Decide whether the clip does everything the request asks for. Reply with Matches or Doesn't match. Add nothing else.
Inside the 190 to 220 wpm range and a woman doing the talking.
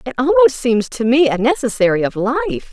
Matches